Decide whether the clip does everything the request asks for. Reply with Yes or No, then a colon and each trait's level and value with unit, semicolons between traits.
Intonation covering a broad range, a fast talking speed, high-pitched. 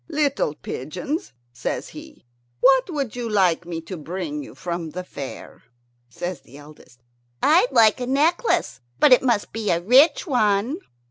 No: wide, 8.8 semitones; average, 155 wpm; high, 205 Hz